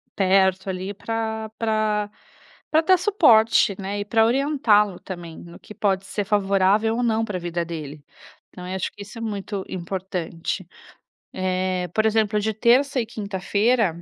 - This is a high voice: Yes, high, 205 Hz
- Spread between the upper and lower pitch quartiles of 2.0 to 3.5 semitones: Yes, average, 2.9 semitones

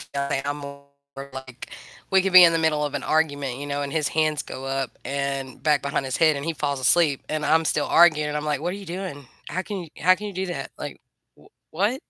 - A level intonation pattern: No, average, 3.3 semitones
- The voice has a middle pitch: Yes, medium, 150 Hz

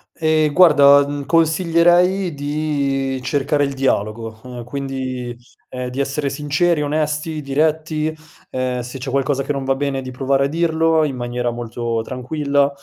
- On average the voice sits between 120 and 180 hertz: Yes, medium, 140 Hz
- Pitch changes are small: No, average, 3.1 semitones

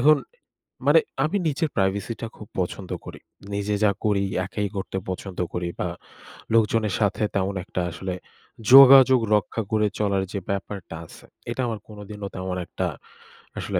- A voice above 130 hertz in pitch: No, low, 105 Hz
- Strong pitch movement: No, average, 2.9 semitones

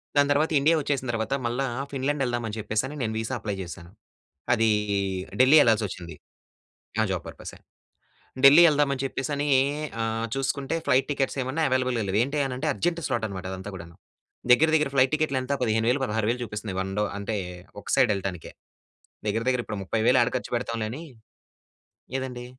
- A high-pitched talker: No, low, 125 Hz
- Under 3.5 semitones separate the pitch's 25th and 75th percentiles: No, average, 4.1 semitones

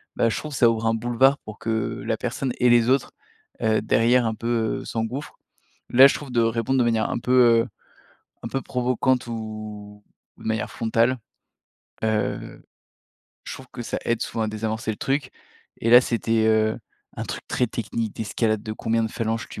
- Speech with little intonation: Yes, narrow, 1.9 semitones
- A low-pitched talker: Yes, low, 115 Hz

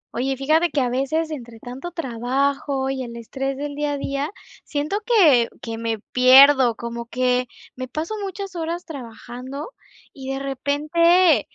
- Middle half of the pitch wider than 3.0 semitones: Yes, average, 3.6 semitones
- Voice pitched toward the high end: Yes, very high, 275 Hz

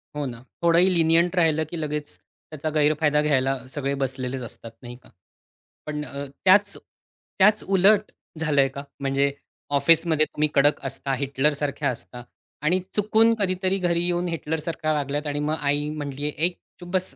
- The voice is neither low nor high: Yes, medium, 150 Hz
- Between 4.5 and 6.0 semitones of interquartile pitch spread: No, average, 3.5 semitones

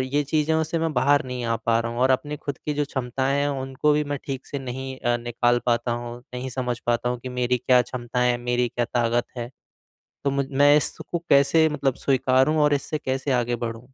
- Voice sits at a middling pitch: No, low, 130 Hz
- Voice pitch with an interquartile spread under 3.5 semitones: Yes, average, 2.7 semitones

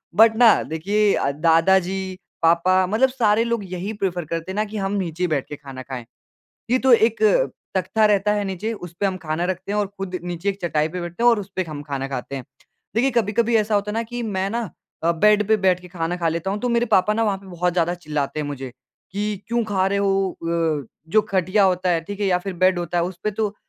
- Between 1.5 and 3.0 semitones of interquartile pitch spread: No, average, 3.7 semitones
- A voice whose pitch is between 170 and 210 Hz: Yes, high, 190 Hz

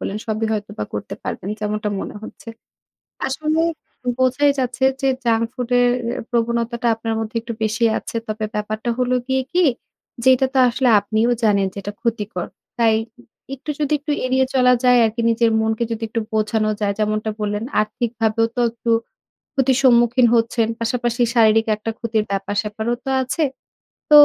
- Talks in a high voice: Yes, high, 230 Hz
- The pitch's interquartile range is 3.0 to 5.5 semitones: No, narrow, 2.6 semitones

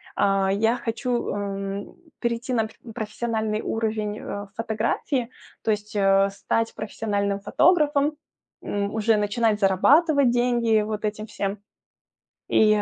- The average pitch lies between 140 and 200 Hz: No, high, 215 Hz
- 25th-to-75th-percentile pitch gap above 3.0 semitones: No, narrow, 2.5 semitones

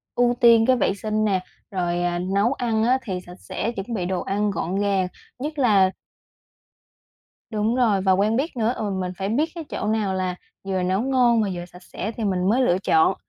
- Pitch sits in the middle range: No, high, 205 Hz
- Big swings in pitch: No, average, 3.8 semitones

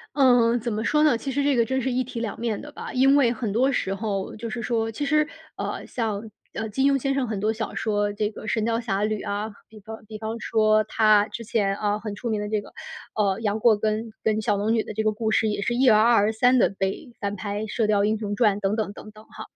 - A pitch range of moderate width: No, narrow, 2.1 semitones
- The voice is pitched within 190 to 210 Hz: No, high, 220 Hz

